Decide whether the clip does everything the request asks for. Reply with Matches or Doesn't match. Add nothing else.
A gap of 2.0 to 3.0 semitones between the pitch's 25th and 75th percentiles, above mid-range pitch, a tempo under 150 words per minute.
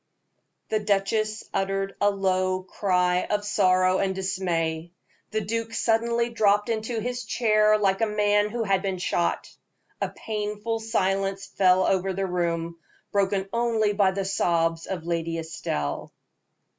Matches